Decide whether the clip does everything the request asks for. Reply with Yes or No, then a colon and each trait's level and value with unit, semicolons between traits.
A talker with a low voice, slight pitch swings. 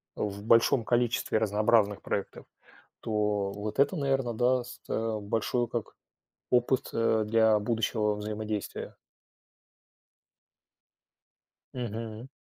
Yes: low, 110 Hz; narrow, 2.2 semitones